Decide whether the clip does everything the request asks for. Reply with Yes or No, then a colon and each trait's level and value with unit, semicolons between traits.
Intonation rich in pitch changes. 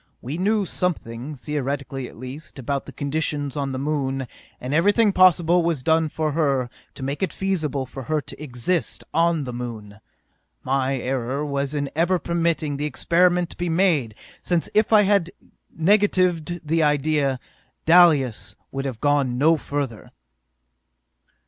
No: average, 4.1 semitones